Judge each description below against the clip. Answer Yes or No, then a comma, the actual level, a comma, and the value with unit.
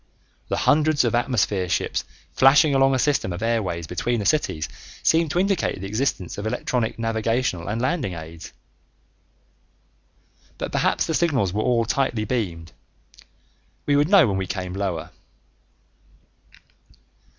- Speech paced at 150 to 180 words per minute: No, average, 140 wpm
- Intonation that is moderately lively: No, wide, 6.5 semitones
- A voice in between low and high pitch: No, low, 115 Hz